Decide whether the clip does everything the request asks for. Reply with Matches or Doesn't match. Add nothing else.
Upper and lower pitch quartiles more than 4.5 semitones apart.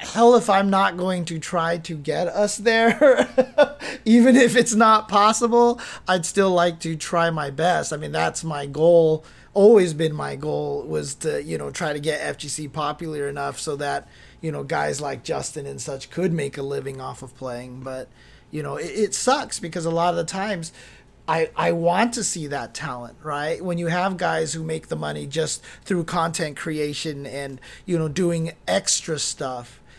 Matches